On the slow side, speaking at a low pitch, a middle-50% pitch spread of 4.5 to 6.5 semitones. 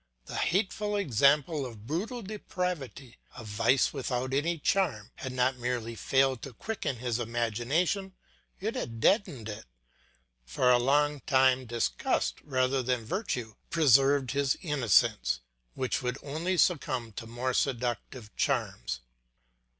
No: slow, 125 wpm; low, 130 Hz; average, 3.9 semitones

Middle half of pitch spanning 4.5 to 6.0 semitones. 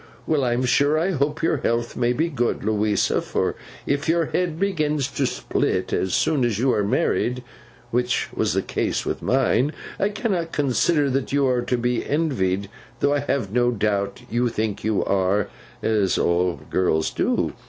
Yes: average, 5.3 semitones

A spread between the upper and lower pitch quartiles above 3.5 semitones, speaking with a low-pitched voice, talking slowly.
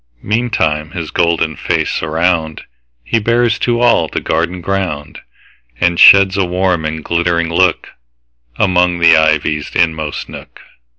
No: average, 3.1 semitones; very low, 85 Hz; slow, 115 wpm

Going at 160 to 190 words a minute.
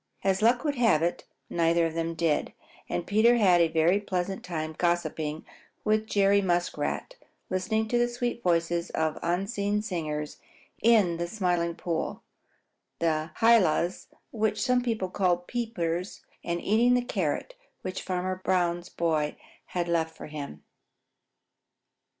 No: average, 140 wpm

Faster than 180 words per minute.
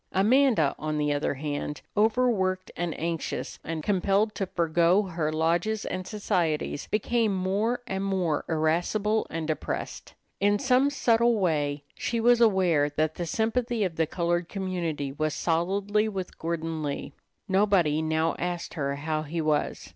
No: average, 145 wpm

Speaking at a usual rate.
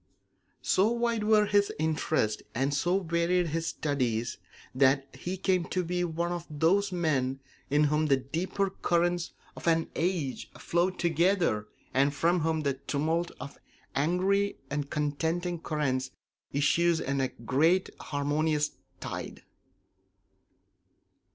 No: slow, 125 wpm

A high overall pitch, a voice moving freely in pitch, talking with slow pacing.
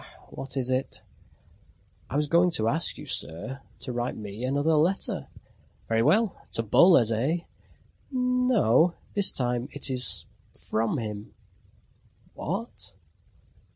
No: low, 135 Hz; wide, 6.8 semitones; slow, 125 wpm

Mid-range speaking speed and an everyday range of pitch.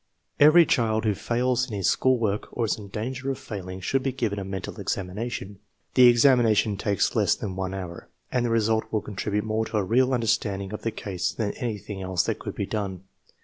No: fast, 225 wpm; average, 3.6 semitones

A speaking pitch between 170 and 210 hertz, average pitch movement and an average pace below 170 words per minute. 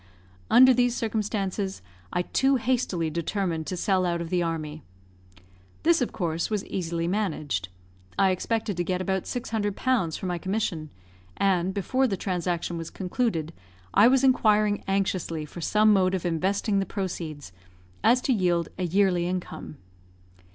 Yes: high, 190 Hz; average, 3.8 semitones; average, 150 wpm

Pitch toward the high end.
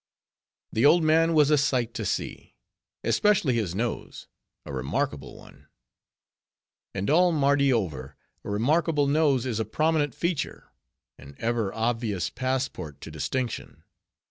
No: low, 130 Hz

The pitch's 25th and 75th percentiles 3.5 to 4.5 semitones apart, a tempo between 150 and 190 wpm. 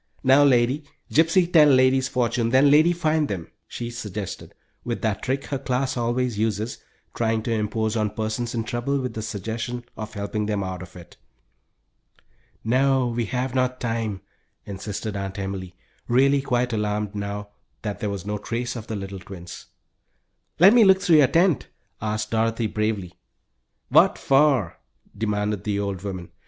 Yes: average, 3.9 semitones; average, 160 wpm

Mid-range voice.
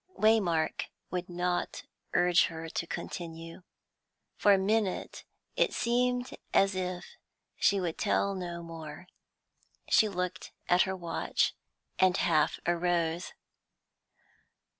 Yes: medium, 180 Hz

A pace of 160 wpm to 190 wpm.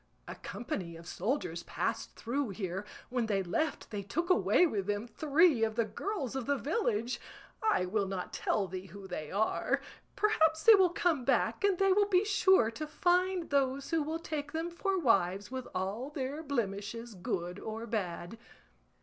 Yes: average, 175 wpm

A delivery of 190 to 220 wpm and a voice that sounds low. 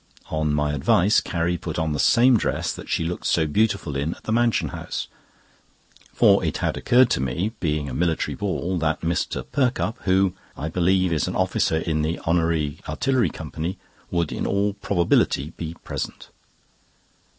No: average, 170 wpm; very low, 85 Hz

